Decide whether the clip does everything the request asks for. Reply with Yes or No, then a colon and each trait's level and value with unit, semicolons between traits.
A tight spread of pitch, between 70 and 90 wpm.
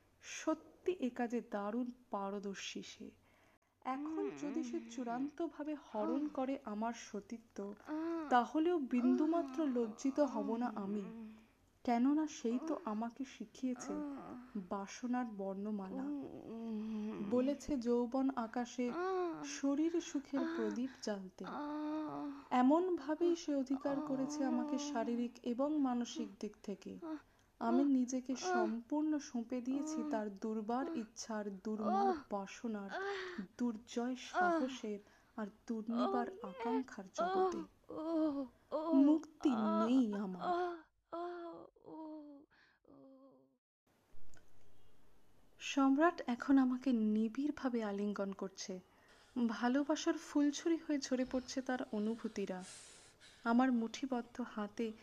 No: average, 5.0 semitones; average, 85 wpm